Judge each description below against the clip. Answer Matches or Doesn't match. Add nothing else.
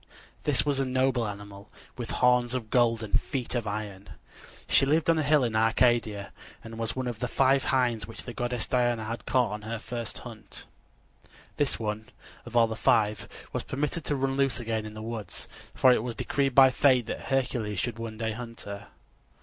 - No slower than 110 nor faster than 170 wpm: Doesn't match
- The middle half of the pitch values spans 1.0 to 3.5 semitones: Matches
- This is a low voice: Matches